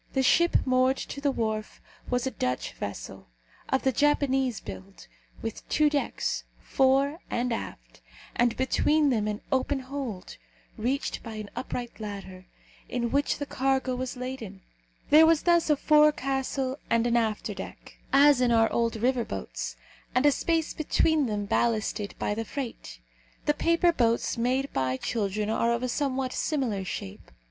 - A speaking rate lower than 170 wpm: Yes, average, 155 wpm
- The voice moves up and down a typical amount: Yes, average, 4.1 semitones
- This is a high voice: Yes, very high, 255 Hz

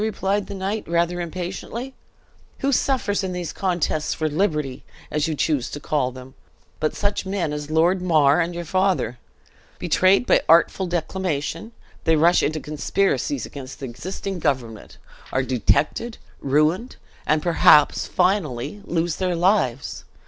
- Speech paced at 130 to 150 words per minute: Yes, average, 140 wpm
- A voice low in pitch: No, medium, 170 Hz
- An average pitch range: Yes, average, 4.3 semitones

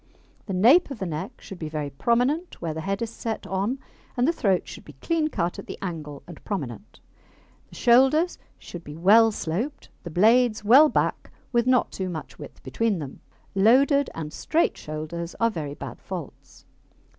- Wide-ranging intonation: Yes, wide, 6.9 semitones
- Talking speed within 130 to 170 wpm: No, average, 180 wpm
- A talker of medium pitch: No, high, 200 Hz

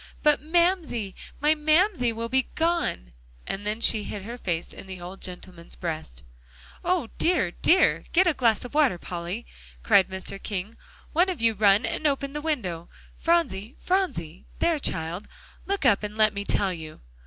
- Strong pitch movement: Yes, wide, 8.5 semitones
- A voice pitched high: Yes, high, 225 Hz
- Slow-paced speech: No, average, 170 wpm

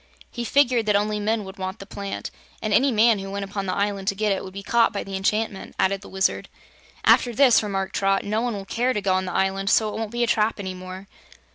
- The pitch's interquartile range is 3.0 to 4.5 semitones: No, narrow, 2.4 semitones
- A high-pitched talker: Yes, high, 205 Hz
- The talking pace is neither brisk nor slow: No, fast, 260 wpm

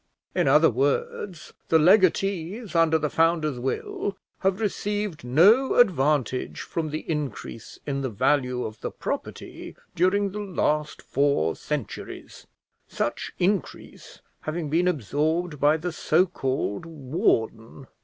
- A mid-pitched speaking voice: Yes, medium, 155 Hz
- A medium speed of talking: No, slow, 125 wpm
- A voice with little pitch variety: No, average, 4.8 semitones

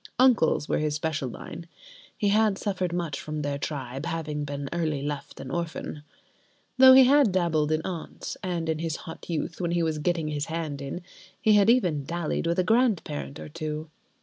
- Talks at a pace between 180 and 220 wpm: Yes, average, 185 wpm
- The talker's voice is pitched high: No, medium, 160 Hz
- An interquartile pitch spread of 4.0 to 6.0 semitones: No, average, 3.2 semitones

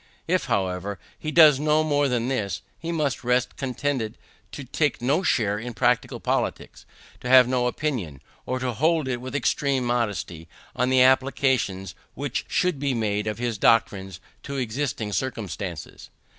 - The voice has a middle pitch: No, low, 125 Hz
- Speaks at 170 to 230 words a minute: No, average, 155 wpm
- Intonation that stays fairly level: No, average, 4.5 semitones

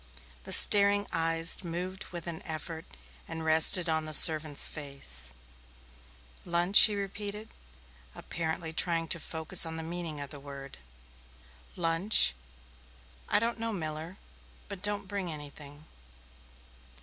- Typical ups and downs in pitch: Yes, average, 3.2 semitones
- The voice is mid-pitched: Yes, medium, 165 Hz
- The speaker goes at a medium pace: No, slow, 125 wpm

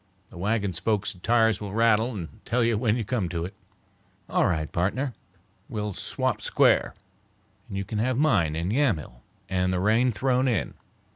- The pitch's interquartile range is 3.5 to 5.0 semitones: Yes, average, 4.2 semitones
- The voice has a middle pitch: No, low, 105 Hz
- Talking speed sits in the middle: Yes, average, 170 wpm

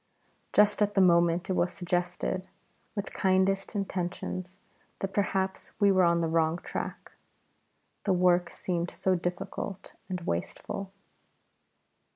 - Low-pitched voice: No, medium, 185 Hz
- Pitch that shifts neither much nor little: No, narrow, 1.8 semitones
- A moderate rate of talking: No, slow, 125 wpm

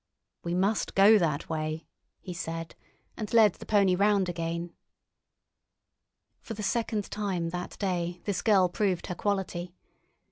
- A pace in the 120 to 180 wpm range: Yes, average, 140 wpm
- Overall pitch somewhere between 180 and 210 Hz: Yes, medium, 185 Hz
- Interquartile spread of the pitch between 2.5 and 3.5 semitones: Yes, average, 3.1 semitones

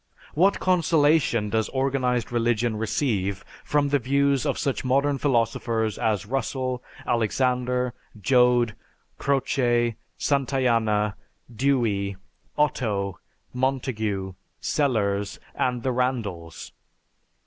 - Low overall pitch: Yes, low, 125 Hz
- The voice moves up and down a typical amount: Yes, average, 3.8 semitones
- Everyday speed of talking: No, slow, 90 wpm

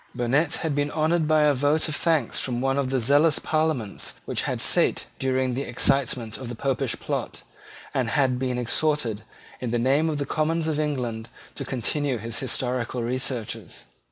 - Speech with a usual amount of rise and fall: Yes, average, 3.5 semitones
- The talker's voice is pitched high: No, low, 135 Hz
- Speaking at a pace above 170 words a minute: Yes, average, 180 wpm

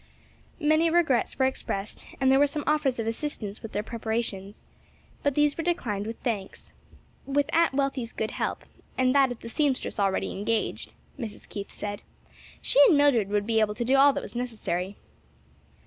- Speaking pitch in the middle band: No, high, 245 Hz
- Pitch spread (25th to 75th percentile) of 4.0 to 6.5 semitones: Yes, average, 5.2 semitones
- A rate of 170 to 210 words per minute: Yes, average, 180 wpm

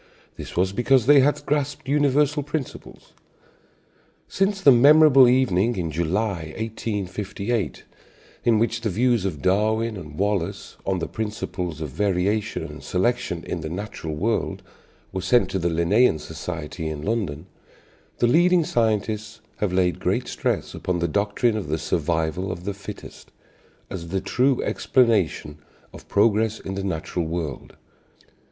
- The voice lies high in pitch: No, low, 100 Hz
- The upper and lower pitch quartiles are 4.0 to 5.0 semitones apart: No, wide, 5.5 semitones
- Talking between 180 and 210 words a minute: No, average, 145 wpm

